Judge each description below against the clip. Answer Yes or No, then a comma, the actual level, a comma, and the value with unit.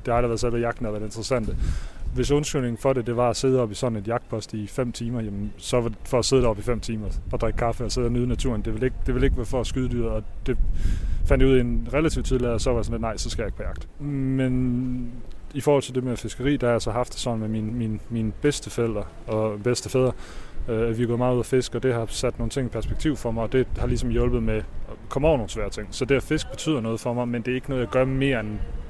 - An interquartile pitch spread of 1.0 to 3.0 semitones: Yes, average, 2.7 semitones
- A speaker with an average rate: No, fast, 305 wpm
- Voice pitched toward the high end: No, low, 120 Hz